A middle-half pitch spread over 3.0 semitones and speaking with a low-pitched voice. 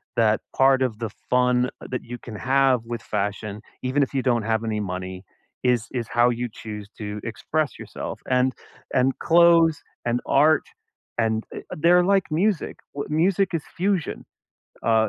Yes: average, 5.2 semitones; low, 125 Hz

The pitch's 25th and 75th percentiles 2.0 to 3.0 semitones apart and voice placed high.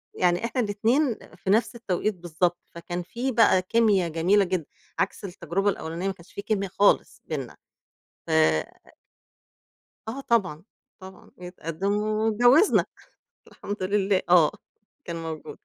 No: average, 3.7 semitones; high, 195 Hz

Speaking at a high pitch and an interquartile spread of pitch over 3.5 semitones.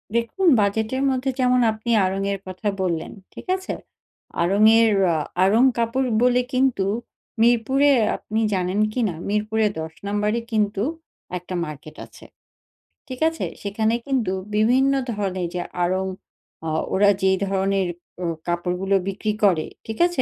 Yes: high, 210 Hz; average, 4.1 semitones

